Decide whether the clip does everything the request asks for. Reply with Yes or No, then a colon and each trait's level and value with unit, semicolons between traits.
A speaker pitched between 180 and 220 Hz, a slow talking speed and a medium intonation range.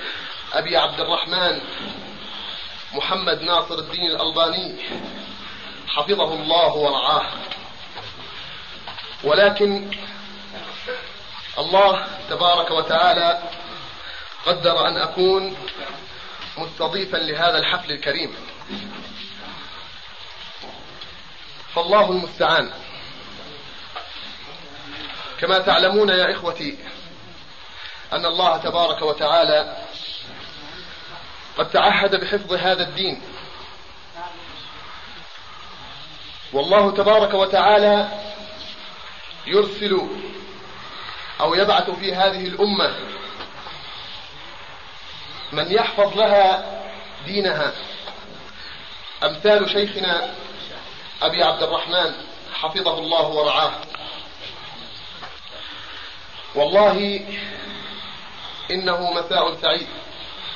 Yes: medium, 185 Hz; slow, 60 wpm; average, 3.6 semitones